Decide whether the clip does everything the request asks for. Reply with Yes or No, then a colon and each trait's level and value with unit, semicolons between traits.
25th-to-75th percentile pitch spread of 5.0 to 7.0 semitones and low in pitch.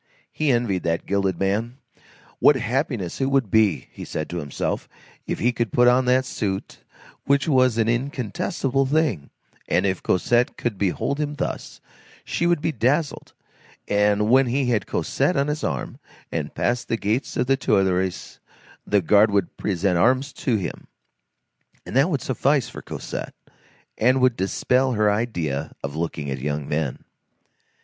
Yes: wide, 5.6 semitones; low, 115 Hz